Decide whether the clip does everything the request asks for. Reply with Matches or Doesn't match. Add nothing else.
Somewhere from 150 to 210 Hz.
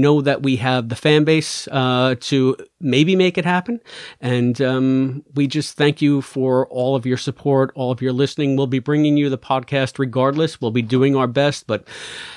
Doesn't match